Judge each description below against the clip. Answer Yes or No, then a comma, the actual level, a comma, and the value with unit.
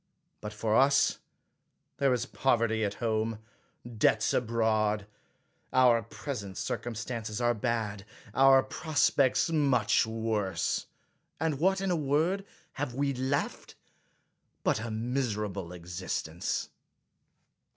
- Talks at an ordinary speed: No, slow, 110 wpm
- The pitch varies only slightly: No, average, 4.1 semitones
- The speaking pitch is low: Yes, low, 115 Hz